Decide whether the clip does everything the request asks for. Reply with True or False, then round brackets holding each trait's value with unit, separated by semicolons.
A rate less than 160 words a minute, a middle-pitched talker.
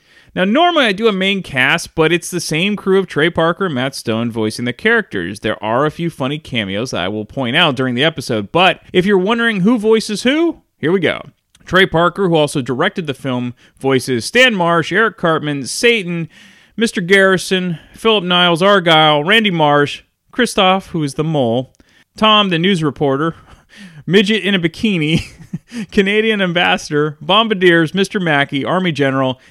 False (170 wpm; 170 Hz)